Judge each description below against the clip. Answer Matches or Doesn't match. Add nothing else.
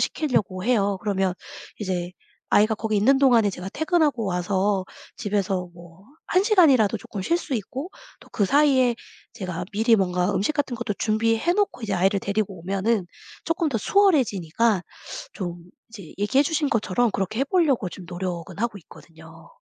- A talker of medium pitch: Doesn't match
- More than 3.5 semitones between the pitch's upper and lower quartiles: Matches